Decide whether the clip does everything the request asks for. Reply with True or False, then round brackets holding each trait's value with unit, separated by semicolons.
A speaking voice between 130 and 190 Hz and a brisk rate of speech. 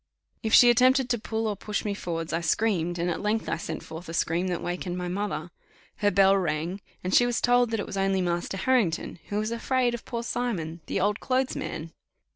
False (200 Hz; 225 wpm)